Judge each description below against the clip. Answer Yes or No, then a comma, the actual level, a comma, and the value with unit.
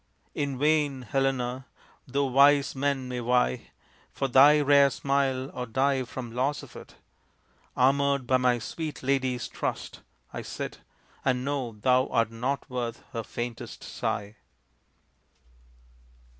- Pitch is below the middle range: Yes, low, 130 Hz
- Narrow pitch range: Yes, narrow, 2.1 semitones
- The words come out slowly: Yes, slow, 130 wpm